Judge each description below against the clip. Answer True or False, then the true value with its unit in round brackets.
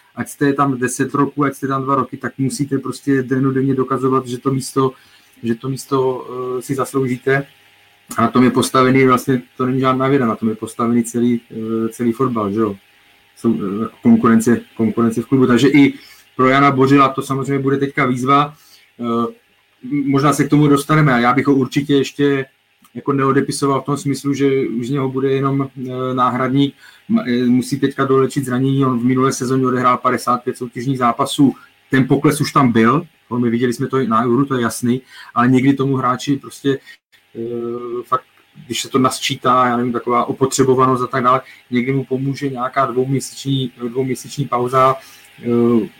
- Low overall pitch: True (130 Hz)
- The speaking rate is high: True (175 wpm)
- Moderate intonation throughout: False (2.0 semitones)